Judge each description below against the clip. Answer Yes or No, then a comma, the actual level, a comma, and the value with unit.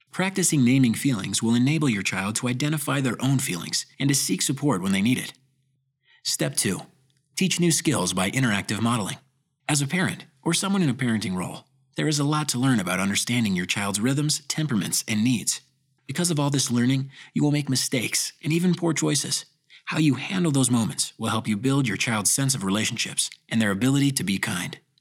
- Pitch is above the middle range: No, low, 135 Hz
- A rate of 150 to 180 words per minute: No, average, 200 wpm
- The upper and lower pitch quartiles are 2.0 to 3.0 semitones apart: No, average, 3.8 semitones